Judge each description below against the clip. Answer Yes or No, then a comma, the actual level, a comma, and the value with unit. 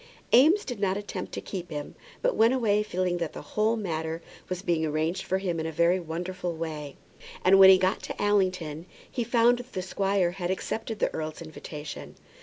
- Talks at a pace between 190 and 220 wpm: Yes, average, 200 wpm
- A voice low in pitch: No, medium, 185 Hz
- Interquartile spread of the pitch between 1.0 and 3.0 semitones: No, average, 4.0 semitones